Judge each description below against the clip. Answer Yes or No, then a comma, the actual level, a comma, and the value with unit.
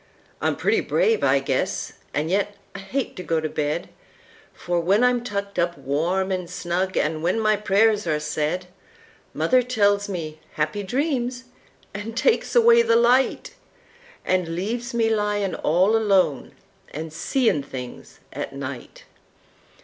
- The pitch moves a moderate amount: No, wide, 5.9 semitones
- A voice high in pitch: Yes, high, 200 Hz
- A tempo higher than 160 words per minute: No, slow, 135 wpm